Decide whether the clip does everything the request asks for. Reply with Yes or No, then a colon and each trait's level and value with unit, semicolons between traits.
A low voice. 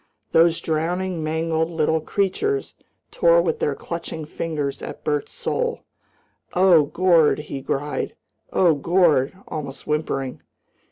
No: medium, 160 Hz